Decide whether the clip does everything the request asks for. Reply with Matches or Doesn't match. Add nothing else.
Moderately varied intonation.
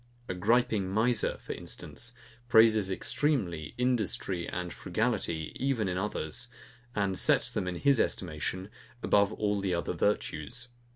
Matches